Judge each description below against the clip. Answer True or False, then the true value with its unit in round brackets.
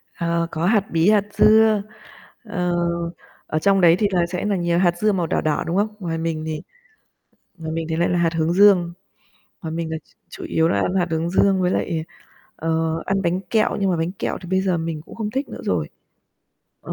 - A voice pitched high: False (175 Hz)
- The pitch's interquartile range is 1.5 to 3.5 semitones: True (3.1 semitones)